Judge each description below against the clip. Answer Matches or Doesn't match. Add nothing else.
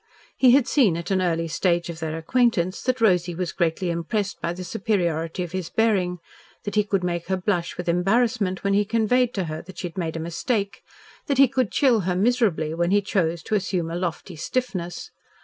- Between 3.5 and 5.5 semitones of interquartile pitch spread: Matches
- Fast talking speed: Matches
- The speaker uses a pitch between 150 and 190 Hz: Matches